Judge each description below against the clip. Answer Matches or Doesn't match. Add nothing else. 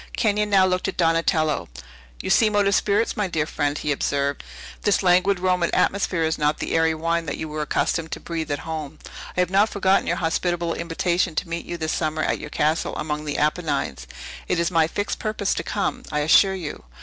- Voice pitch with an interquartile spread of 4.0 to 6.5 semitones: Doesn't match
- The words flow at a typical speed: Doesn't match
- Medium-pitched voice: Matches